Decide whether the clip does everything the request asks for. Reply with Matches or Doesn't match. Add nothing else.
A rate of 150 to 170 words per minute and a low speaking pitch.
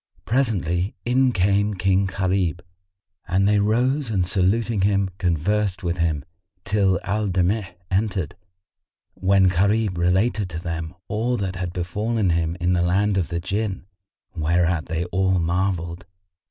Doesn't match